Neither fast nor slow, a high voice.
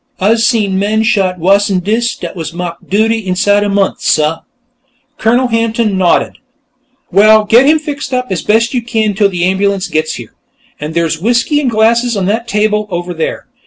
Yes: average, 180 wpm; high, 210 Hz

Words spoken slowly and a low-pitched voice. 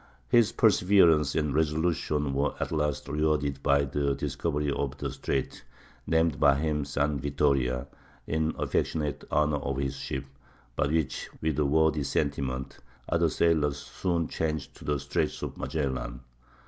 No: average, 145 wpm; very low, 75 Hz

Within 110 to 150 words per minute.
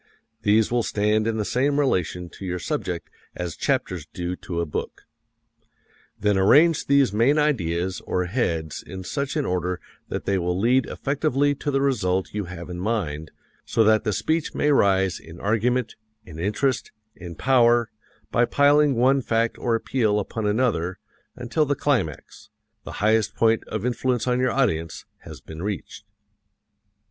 No: average, 160 wpm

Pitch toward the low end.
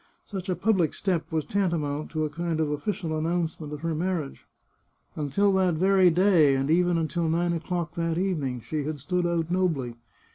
No: medium, 165 Hz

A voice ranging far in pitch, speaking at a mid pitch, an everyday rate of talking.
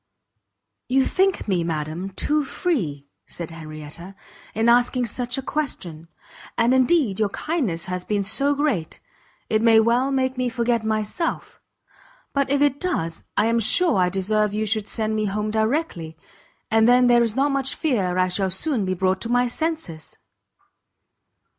No: wide, 5.9 semitones; high, 220 Hz; average, 160 wpm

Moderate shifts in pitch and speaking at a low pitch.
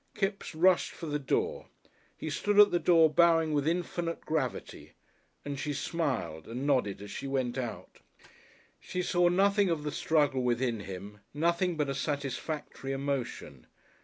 No: average, 4.7 semitones; medium, 150 Hz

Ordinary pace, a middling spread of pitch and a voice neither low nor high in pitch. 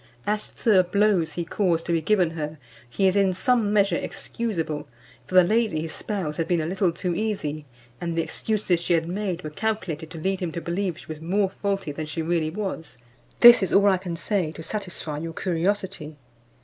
No: fast, 210 wpm; average, 3.7 semitones; medium, 175 Hz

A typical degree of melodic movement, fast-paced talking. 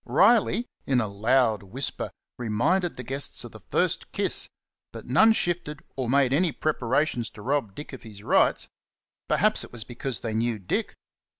No: average, 4.8 semitones; average, 170 wpm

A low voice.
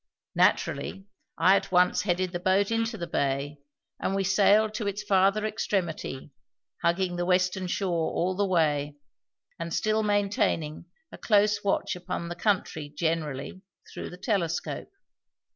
No: medium, 185 Hz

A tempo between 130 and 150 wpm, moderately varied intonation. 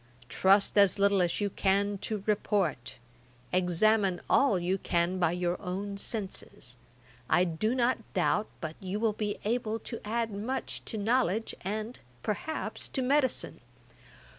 Yes: average, 140 wpm; average, 3.3 semitones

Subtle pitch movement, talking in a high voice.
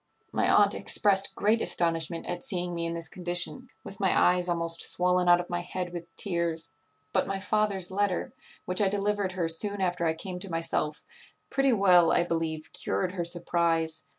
No: narrow, 2.3 semitones; medium, 175 Hz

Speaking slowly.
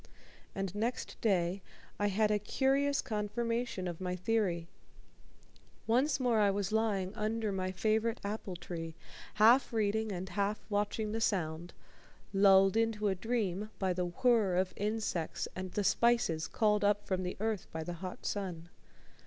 No: average, 155 wpm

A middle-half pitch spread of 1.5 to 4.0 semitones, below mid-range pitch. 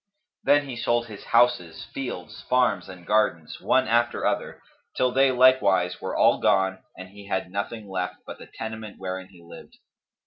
No: average, 4.6 semitones; low, 105 Hz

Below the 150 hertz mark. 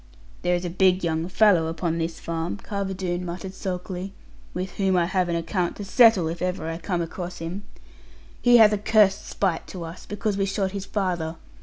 No: medium, 185 Hz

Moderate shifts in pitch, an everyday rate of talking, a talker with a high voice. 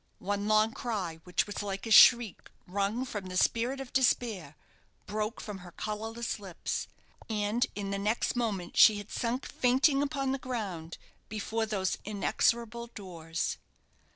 Yes: average, 3.2 semitones; average, 150 wpm; high, 215 Hz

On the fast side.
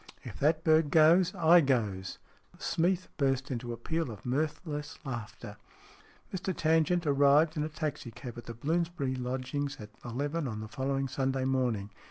No: average, 165 wpm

